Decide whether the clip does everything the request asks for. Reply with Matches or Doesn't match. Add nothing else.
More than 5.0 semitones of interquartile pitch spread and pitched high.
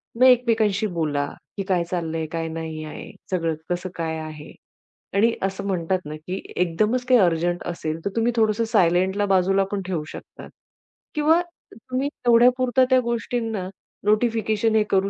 Matches